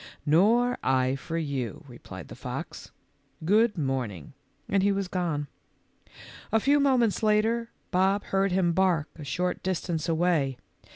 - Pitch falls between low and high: Yes, medium, 180 Hz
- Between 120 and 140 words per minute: Yes, slow, 135 wpm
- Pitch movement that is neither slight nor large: No, wide, 5.8 semitones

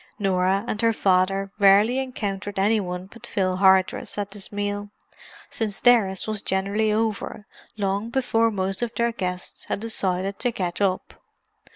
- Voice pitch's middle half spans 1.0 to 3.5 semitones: Yes, narrow, 2.5 semitones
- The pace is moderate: Yes, average, 155 wpm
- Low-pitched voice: No, high, 200 Hz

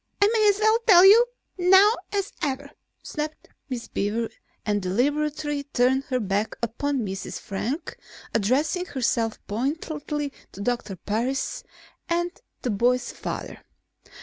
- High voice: Yes, very high, 270 Hz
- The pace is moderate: No, slow, 125 wpm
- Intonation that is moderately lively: No, wide, 5.8 semitones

